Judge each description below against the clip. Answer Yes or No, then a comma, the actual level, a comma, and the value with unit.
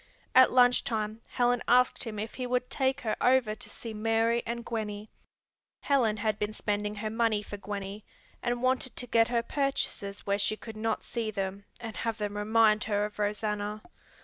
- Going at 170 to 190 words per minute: Yes, average, 185 wpm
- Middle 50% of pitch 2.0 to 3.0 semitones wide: Yes, narrow, 2.4 semitones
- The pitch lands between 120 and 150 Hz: No, high, 220 Hz